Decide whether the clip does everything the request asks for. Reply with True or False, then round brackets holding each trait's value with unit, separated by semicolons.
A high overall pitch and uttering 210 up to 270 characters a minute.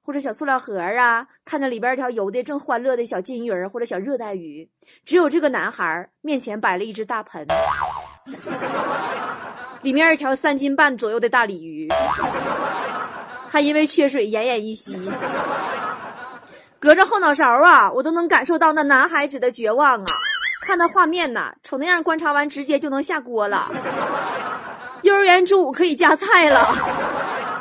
True (275 Hz; 250 characters per minute)